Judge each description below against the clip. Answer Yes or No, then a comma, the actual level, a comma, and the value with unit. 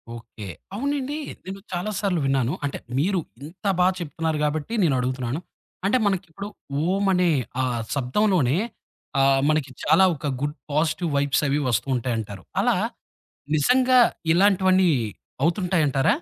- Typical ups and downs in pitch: No, wide, 5.7 semitones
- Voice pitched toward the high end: No, medium, 160 Hz